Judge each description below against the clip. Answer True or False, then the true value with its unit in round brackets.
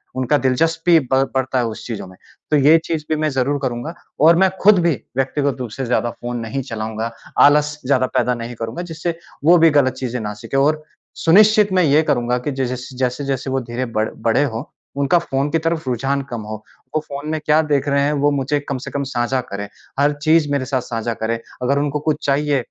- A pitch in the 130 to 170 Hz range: True (135 Hz)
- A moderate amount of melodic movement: True (3.5 semitones)